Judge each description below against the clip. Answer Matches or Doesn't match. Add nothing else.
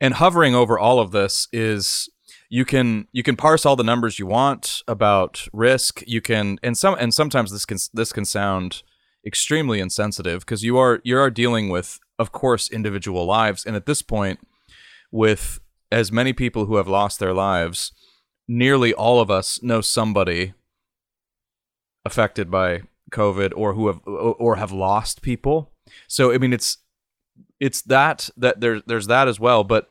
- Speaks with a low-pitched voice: Matches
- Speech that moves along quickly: Doesn't match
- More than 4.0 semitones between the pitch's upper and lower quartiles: Doesn't match